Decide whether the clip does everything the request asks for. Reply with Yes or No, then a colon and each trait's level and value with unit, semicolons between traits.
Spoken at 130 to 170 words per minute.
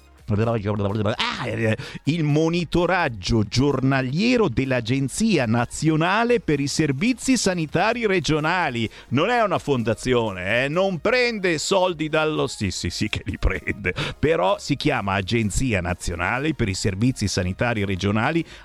No: slow, 115 wpm